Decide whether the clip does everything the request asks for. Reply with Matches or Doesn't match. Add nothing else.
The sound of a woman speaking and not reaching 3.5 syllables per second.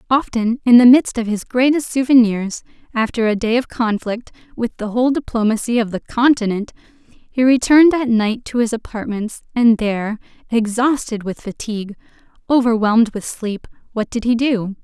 Doesn't match